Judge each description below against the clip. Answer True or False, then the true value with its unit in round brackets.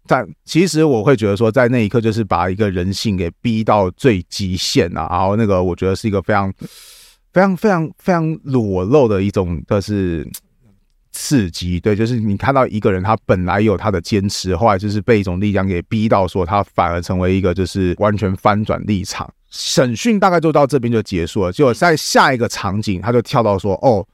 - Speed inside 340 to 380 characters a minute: False (305 characters per minute)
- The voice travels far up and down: False (3.9 semitones)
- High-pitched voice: False (105 Hz)